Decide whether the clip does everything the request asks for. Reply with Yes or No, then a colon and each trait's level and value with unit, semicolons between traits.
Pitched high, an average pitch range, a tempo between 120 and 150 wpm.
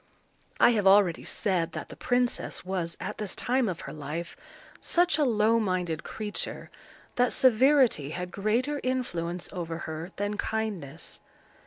No: high, 205 Hz; wide, 6.0 semitones; average, 145 wpm